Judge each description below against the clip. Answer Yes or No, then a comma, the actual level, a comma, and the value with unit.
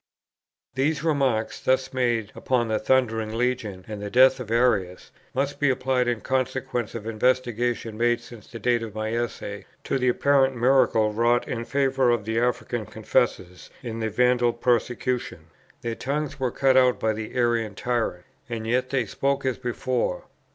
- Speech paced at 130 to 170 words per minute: Yes, average, 165 wpm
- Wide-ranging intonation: No, average, 2.7 semitones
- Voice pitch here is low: Yes, low, 120 Hz